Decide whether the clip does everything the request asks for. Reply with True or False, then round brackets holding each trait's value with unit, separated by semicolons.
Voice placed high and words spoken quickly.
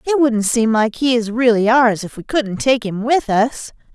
True (235 Hz; 230 wpm)